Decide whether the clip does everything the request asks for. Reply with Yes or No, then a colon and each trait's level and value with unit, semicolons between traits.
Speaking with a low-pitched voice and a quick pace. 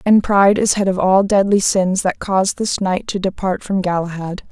No: high, 190 Hz; fast, 215 wpm